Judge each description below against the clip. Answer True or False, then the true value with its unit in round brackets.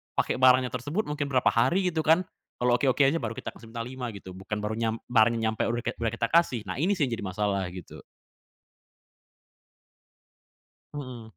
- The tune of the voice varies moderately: True (3.9 semitones)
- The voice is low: True (120 Hz)